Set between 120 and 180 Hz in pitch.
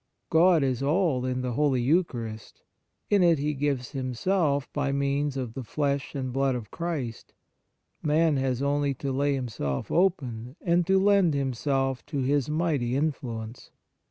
Yes: medium, 140 Hz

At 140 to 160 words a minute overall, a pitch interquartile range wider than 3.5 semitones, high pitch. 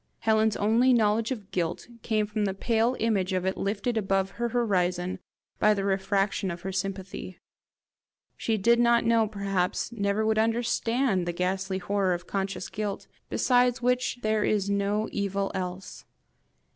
No: average, 155 wpm; average, 2.8 semitones; high, 205 Hz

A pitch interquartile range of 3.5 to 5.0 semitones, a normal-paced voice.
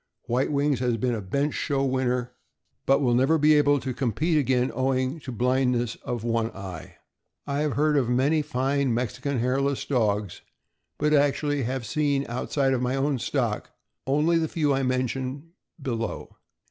No: average, 2.7 semitones; average, 165 wpm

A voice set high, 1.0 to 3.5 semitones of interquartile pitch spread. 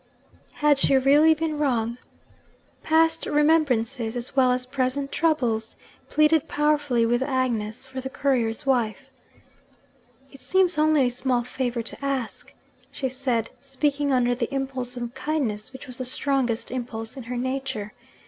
Yes: very high, 260 Hz; average, 2.8 semitones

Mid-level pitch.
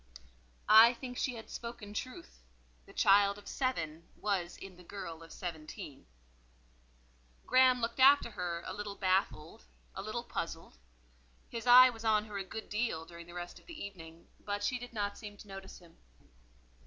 No: high, 205 Hz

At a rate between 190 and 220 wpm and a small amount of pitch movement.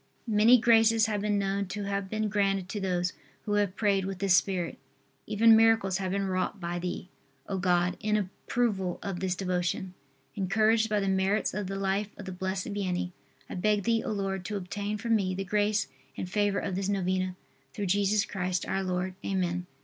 Yes: average, 195 wpm; narrow, 2.0 semitones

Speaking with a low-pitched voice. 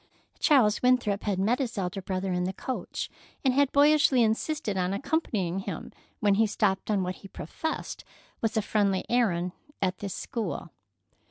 No: high, 210 Hz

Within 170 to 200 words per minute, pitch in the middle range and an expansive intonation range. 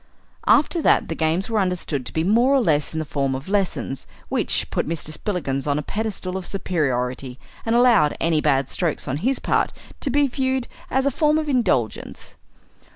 Yes: average, 190 wpm; medium, 180 Hz; wide, 8.7 semitones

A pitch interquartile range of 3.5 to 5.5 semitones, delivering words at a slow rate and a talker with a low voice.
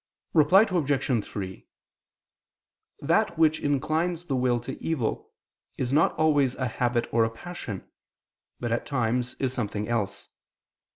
Yes: average, 4.8 semitones; slow, 130 wpm; low, 130 Hz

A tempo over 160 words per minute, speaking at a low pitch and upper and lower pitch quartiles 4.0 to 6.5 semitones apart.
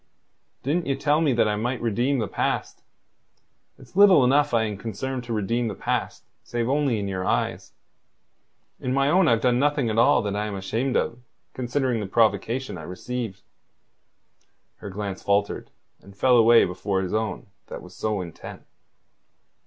Yes: average, 170 wpm; low, 115 Hz; average, 4.3 semitones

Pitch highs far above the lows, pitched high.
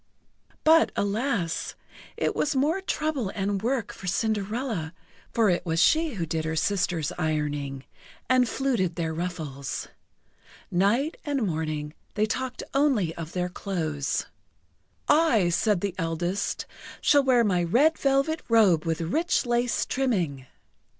Yes: wide, 7.8 semitones; high, 200 Hz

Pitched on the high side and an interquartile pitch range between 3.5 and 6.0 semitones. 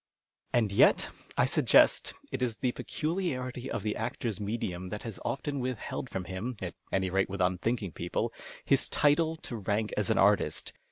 No: low, 110 Hz; average, 4.7 semitones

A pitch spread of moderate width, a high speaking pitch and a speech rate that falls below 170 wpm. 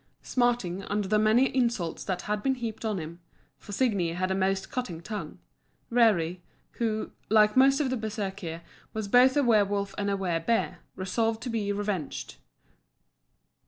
Yes: average, 3.6 semitones; high, 210 Hz; average, 160 wpm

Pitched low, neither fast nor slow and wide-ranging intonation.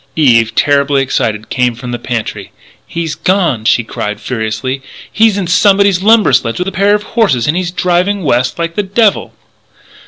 No: medium, 160 Hz; average, 175 wpm; wide, 8.4 semitones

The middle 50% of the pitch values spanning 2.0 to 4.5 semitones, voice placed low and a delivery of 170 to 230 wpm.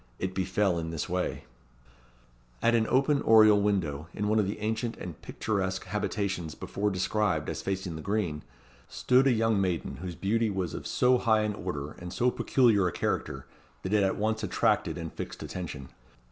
Yes: average, 3.4 semitones; low, 100 Hz; average, 180 wpm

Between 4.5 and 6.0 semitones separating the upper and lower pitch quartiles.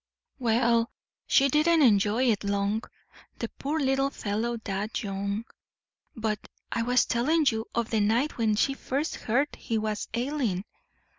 No: average, 4.1 semitones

